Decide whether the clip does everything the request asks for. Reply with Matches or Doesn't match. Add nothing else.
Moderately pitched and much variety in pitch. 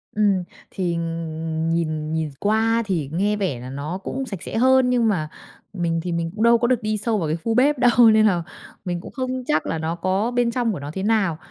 Doesn't match